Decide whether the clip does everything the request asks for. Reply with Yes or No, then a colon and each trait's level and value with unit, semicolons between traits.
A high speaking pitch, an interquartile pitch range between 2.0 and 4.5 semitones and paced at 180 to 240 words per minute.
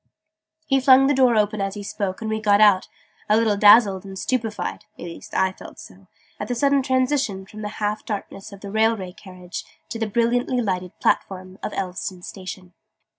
Yes: high, 210 Hz; average, 3.5 semitones; average, 190 wpm